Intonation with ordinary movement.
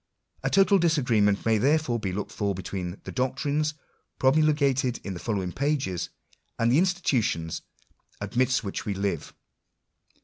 No: wide, 6.6 semitones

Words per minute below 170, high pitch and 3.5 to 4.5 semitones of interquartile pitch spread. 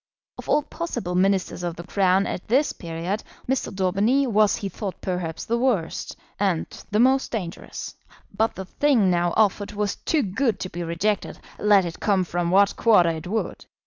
No: average, 175 wpm; high, 195 Hz; average, 3.8 semitones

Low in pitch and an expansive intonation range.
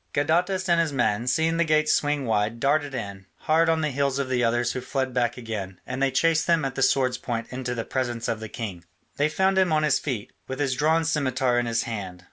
No: low, 130 Hz; average, 4.5 semitones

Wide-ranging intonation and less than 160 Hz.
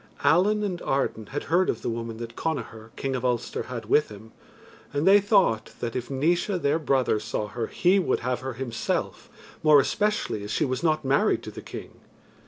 Yes: wide, 6.5 semitones; low, 135 Hz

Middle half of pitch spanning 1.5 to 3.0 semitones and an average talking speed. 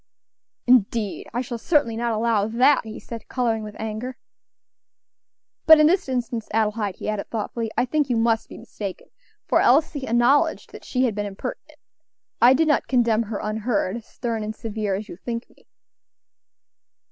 Yes: average, 2.7 semitones; average, 165 wpm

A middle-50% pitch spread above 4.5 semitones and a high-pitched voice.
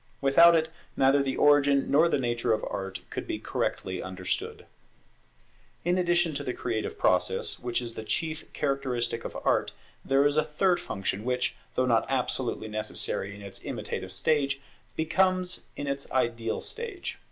No: average, 5.2 semitones; low, 135 Hz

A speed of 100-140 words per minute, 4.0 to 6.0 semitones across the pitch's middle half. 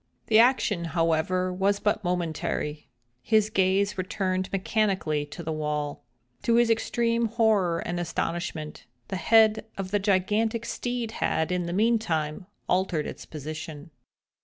Yes: slow, 135 wpm; average, 4.7 semitones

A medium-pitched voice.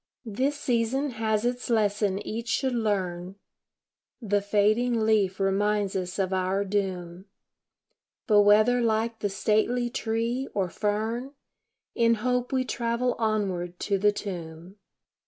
No: high, 215 Hz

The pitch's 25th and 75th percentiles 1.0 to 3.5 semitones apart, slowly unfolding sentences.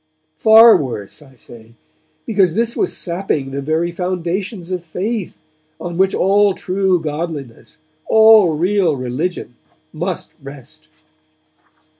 No: average, 5.0 semitones; slow, 115 wpm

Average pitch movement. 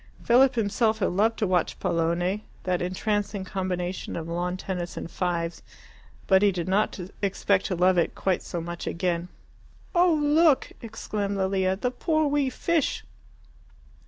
Yes: average, 3.9 semitones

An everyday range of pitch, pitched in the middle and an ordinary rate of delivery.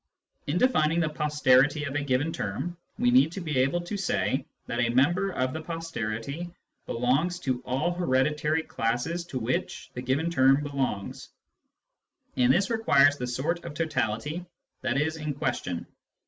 Yes: average, 4.4 semitones; medium, 145 Hz; average, 160 wpm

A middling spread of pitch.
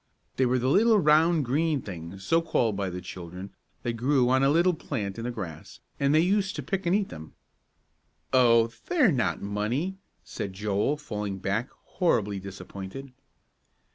No: wide, 8.0 semitones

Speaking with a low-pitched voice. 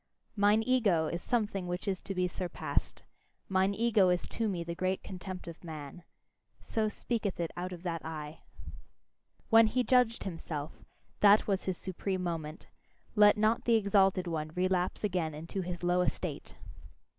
No: medium, 185 Hz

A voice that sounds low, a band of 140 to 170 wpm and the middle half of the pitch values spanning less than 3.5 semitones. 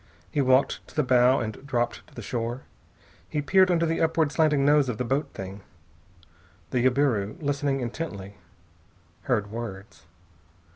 No: low, 130 Hz; average, 150 wpm; average, 4.2 semitones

